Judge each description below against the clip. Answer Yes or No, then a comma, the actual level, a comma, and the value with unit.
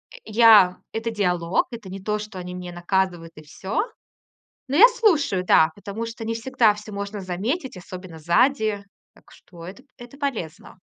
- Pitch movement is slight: No, average, 4.1 semitones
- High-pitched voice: Yes, high, 205 Hz